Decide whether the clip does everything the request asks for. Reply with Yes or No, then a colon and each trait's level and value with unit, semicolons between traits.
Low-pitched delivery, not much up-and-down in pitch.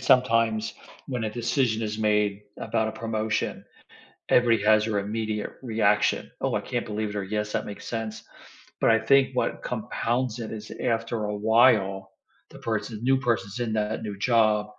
Yes: low, 110 Hz; narrow, 1.6 semitones